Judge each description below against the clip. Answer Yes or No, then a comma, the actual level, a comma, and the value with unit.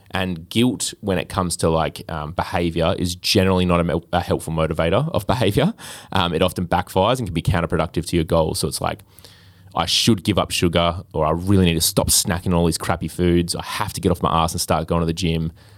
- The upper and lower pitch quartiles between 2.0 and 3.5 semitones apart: Yes, narrow, 2.5 semitones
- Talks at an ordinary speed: No, fast, 235 wpm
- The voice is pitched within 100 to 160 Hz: No, very low, 90 Hz